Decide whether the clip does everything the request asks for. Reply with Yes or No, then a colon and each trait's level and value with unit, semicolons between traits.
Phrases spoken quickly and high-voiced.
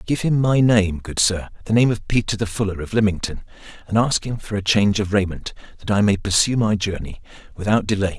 No: fast, 220 wpm; low, 100 Hz